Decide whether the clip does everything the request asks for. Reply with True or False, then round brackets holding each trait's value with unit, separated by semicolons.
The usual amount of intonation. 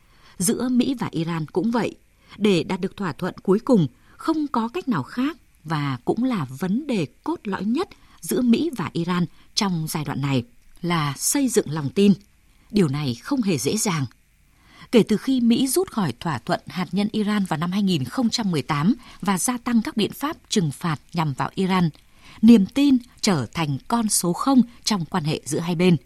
False (6.6 semitones)